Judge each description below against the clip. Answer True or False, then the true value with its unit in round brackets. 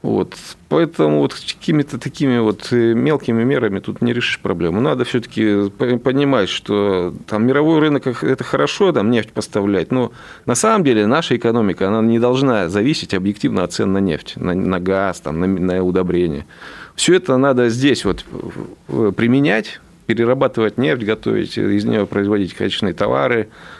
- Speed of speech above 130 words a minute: True (155 wpm)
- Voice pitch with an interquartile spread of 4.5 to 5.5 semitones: True (4.8 semitones)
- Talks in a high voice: False (110 Hz)